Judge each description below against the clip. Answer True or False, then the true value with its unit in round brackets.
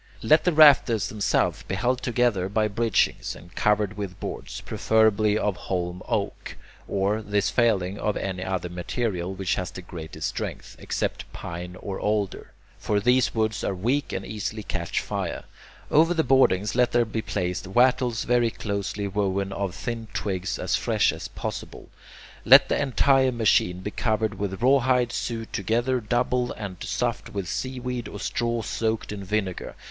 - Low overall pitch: True (105 Hz)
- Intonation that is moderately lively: True (3.9 semitones)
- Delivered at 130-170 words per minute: True (160 wpm)